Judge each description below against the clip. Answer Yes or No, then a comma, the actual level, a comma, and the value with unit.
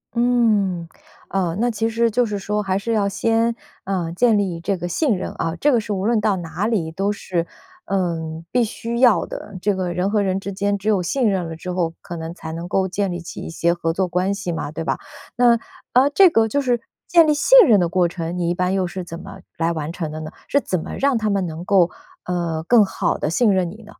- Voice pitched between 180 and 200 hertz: Yes, high, 190 Hz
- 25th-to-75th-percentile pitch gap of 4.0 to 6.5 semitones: Yes, average, 4.5 semitones